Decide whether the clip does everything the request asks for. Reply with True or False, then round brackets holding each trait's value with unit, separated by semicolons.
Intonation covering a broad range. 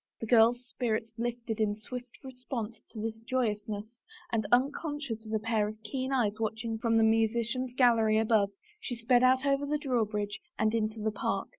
False (2.4 semitones)